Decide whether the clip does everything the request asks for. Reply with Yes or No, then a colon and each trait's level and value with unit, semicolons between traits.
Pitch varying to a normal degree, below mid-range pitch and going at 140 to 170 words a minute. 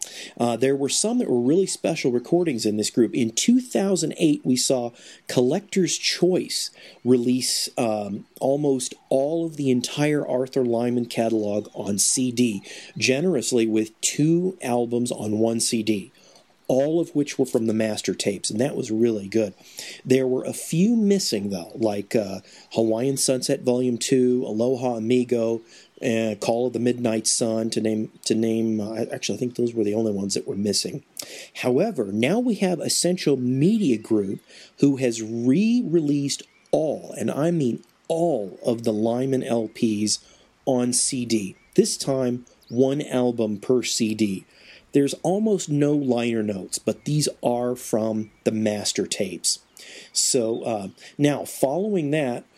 Yes: average, 4.2 semitones; low, 125 Hz; average, 150 wpm